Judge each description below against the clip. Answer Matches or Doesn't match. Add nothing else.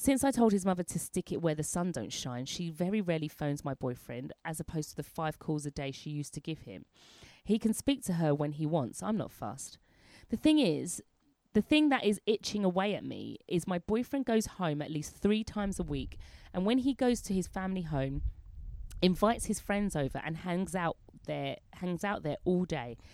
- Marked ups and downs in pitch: Matches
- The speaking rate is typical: Doesn't match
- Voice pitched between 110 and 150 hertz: Doesn't match